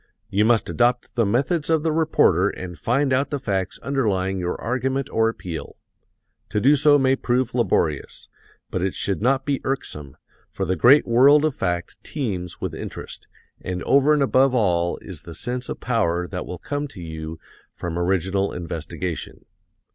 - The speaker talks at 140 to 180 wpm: Yes, average, 170 wpm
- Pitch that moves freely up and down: Yes, wide, 7.1 semitones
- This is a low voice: Yes, low, 115 Hz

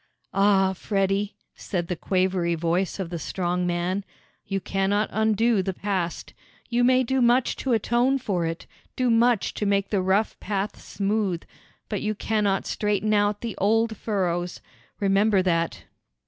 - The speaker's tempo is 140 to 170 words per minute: Yes, average, 150 wpm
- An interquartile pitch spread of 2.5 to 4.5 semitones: Yes, average, 2.9 semitones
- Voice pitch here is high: Yes, high, 200 Hz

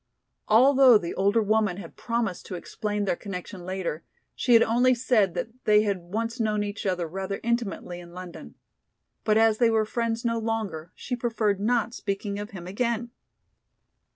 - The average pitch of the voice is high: Yes, high, 210 Hz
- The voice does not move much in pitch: No, average, 3.3 semitones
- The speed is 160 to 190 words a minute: Yes, average, 170 wpm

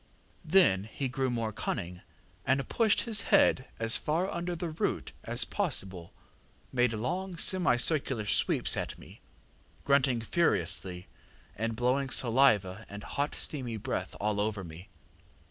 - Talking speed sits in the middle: No, slow, 130 wpm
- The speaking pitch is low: Yes, low, 125 Hz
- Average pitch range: No, wide, 6.1 semitones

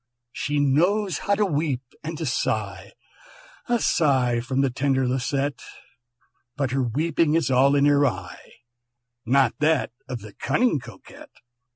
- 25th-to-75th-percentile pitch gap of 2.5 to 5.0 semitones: Yes, average, 3.5 semitones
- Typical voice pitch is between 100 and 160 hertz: Yes, medium, 140 Hz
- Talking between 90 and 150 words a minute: Yes, average, 145 wpm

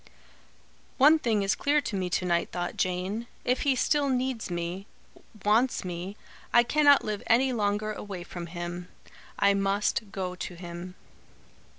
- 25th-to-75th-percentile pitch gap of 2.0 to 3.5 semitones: No, average, 5.1 semitones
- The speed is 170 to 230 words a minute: No, average, 155 wpm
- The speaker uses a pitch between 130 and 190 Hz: No, high, 200 Hz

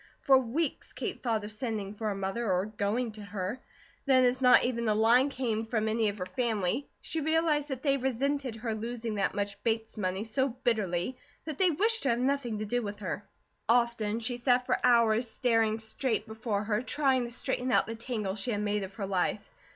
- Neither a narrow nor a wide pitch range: Yes, average, 3.3 semitones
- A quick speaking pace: Yes, fast, 210 wpm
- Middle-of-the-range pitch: No, high, 230 Hz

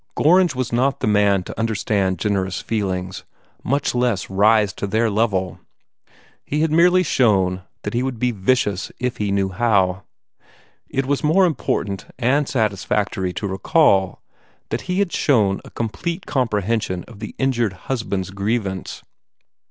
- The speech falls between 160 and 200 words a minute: No, average, 150 wpm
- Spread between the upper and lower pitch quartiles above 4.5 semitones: Yes, average, 4.9 semitones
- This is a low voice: Yes, low, 110 Hz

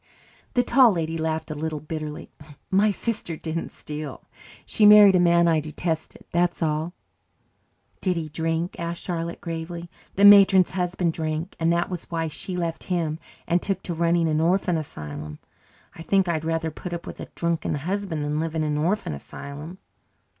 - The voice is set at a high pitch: No, medium, 165 Hz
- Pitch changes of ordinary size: No, narrow, 2.2 semitones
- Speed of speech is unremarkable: Yes, average, 175 wpm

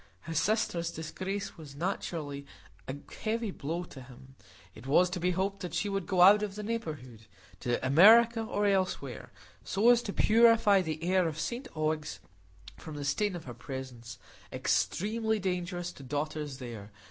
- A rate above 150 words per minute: Yes, average, 160 wpm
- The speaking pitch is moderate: Yes, medium, 175 Hz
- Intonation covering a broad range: Yes, wide, 6.2 semitones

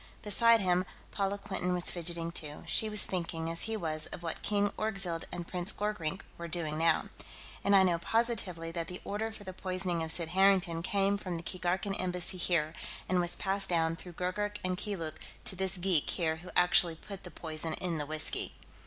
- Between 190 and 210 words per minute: Yes, average, 195 wpm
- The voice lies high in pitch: No, medium, 180 Hz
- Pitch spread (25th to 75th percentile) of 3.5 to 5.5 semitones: No, average, 2.9 semitones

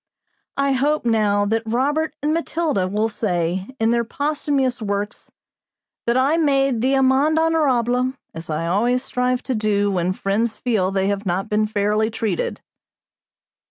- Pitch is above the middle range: Yes, high, 230 Hz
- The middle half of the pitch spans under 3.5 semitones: No, average, 5.0 semitones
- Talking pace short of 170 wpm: Yes, average, 150 wpm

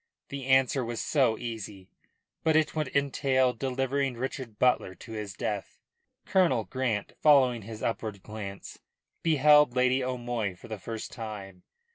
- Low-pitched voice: Yes, low, 125 Hz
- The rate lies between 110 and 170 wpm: Yes, average, 140 wpm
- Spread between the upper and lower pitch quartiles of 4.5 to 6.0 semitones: No, average, 3.6 semitones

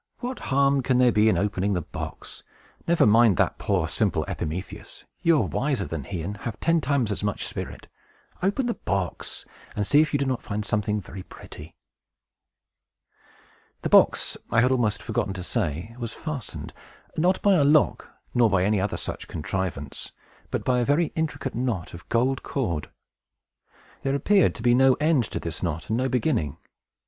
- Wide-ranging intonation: Yes, wide, 6.3 semitones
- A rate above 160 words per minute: Yes, average, 180 wpm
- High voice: No, low, 115 Hz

